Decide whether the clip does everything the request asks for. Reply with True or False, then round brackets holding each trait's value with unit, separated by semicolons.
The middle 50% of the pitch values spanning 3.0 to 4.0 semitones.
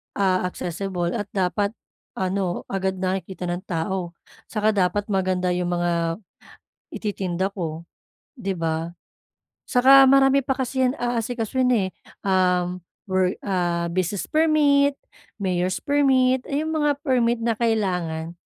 False (5.6 semitones)